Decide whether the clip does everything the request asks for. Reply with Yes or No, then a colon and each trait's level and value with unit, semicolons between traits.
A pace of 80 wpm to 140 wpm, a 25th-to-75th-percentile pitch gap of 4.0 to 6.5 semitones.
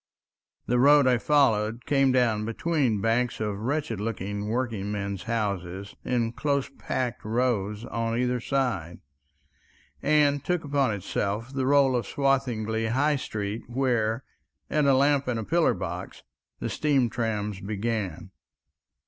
Yes: slow, 135 wpm; average, 4.4 semitones